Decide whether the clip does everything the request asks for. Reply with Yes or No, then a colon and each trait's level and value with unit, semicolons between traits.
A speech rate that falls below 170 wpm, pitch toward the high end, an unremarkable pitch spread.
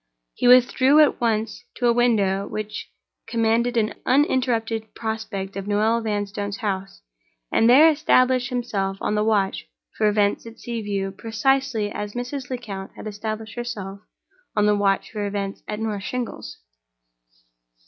Yes: average, 145 wpm; high, 220 Hz; average, 3.0 semitones